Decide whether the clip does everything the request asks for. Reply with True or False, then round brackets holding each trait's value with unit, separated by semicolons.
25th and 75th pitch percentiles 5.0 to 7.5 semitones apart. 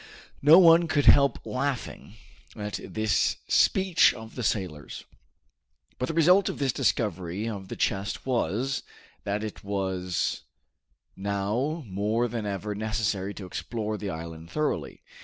True (5.3 semitones)